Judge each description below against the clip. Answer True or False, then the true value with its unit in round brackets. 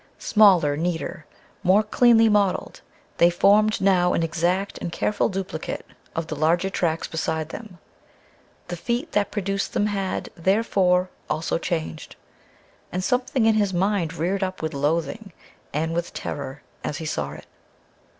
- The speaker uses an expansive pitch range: False (3.9 semitones)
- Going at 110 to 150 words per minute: True (145 wpm)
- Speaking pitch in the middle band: True (180 Hz)